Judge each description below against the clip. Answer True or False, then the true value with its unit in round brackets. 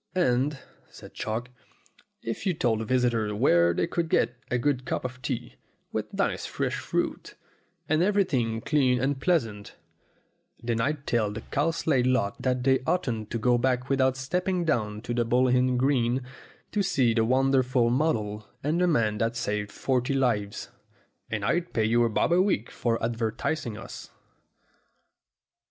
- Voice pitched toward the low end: True (125 Hz)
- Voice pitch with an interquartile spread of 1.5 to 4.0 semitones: True (3.3 semitones)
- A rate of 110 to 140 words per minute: False (160 wpm)